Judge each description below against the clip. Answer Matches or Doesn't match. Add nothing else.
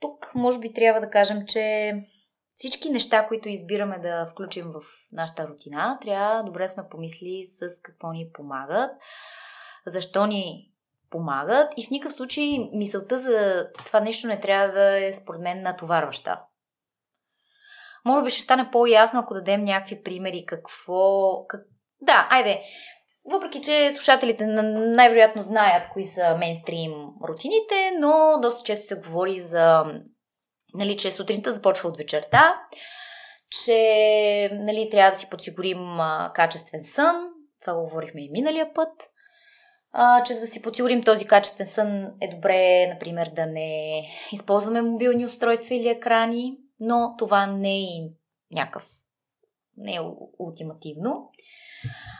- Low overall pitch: Doesn't match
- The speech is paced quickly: Doesn't match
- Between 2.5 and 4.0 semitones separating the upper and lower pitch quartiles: Doesn't match